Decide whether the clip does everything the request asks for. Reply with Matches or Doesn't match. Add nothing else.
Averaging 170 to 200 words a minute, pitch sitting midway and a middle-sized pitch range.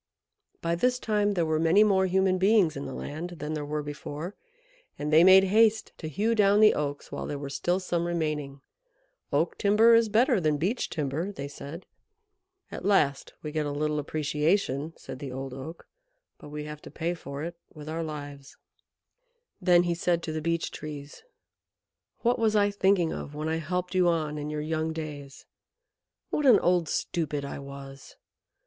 Matches